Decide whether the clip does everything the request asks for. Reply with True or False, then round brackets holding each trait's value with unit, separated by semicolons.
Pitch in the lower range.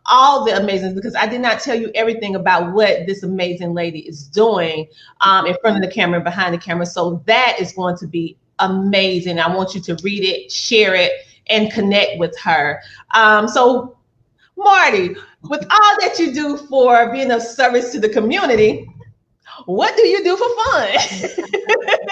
False (215 Hz)